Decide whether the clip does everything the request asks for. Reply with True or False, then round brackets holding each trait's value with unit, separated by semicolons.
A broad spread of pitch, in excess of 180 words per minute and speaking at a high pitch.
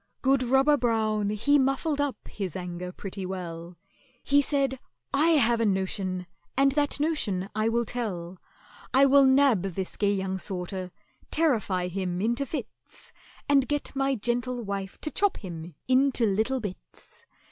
False (6.2 semitones; 150 wpm; 225 Hz)